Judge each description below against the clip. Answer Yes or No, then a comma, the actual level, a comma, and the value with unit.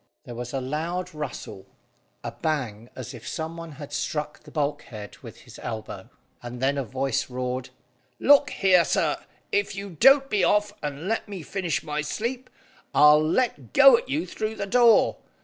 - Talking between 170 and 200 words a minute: Yes, average, 175 wpm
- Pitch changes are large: Yes, wide, 7.5 semitones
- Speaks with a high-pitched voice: No, medium, 155 Hz